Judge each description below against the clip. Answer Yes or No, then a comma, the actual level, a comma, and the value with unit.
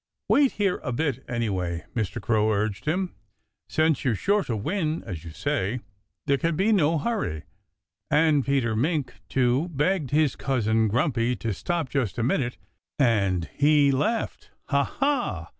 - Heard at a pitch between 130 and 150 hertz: Yes, low, 135 Hz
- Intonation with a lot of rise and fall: Yes, wide, 6.2 semitones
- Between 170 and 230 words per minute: No, average, 155 wpm